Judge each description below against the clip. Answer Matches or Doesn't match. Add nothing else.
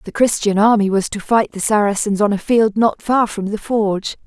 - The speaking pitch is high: Matches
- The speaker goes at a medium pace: Doesn't match